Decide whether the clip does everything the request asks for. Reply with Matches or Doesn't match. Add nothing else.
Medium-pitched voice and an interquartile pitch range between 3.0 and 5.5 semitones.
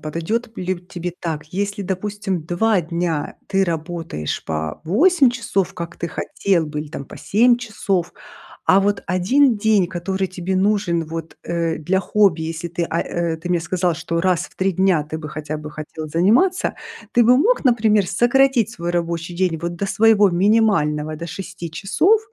Matches